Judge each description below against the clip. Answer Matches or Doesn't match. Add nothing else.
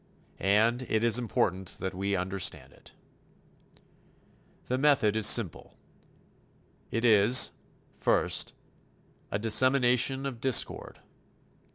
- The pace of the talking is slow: Matches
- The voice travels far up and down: Doesn't match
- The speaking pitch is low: Matches